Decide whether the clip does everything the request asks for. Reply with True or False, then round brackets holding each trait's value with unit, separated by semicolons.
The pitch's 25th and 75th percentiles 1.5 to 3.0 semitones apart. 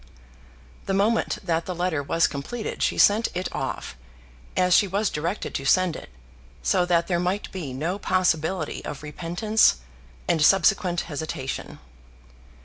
False (3.4 semitones)